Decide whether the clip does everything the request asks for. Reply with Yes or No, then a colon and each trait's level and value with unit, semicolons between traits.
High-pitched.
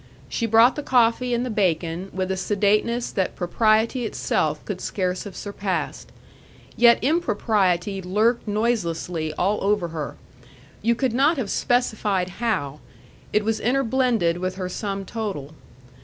Yes: high, 210 Hz